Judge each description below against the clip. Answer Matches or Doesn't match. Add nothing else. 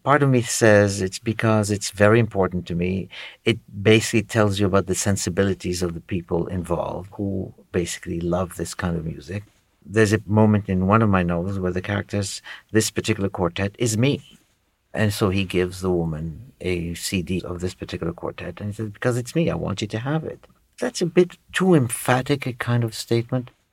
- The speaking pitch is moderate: Doesn't match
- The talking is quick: Doesn't match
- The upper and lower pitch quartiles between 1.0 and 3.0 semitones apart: Doesn't match